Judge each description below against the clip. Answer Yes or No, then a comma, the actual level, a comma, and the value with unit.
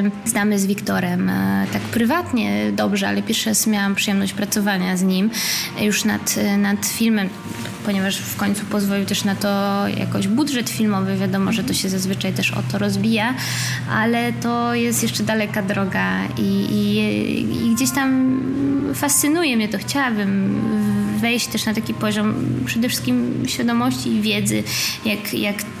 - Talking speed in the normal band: Yes, average, 150 wpm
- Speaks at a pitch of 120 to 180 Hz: No, high, 200 Hz